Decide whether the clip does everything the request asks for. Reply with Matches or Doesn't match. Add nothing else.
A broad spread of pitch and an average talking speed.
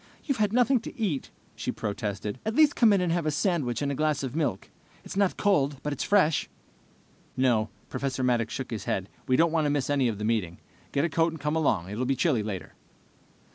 Doesn't match